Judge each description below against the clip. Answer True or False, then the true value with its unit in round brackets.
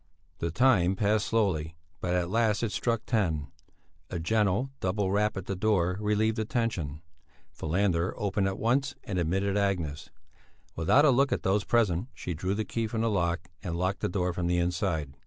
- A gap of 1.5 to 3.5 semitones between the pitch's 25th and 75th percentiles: False (4.0 semitones)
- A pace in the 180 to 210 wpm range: True (185 wpm)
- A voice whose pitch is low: True (95 Hz)